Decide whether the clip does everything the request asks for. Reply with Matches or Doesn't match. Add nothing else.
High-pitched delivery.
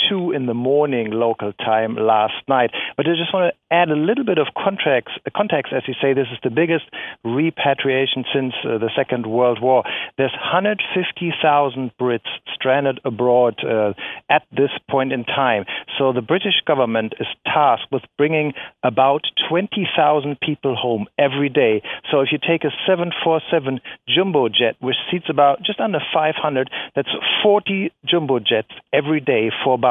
Doesn't match